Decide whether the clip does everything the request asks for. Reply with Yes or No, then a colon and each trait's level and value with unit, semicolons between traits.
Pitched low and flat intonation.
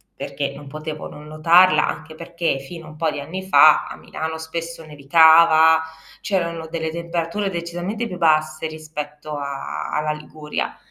No: medium, 160 Hz; narrow, 1.8 semitones